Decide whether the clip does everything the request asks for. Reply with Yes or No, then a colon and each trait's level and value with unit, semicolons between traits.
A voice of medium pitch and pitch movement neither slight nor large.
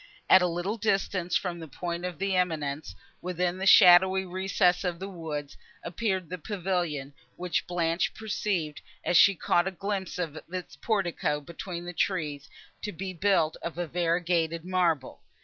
No: medium, 175 Hz; narrow, 2.2 semitones